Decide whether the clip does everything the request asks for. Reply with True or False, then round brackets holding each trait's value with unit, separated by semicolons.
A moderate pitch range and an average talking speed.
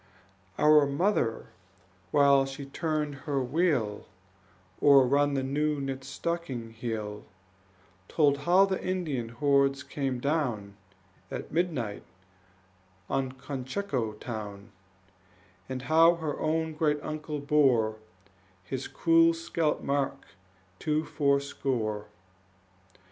False (3.5 semitones; 100 wpm)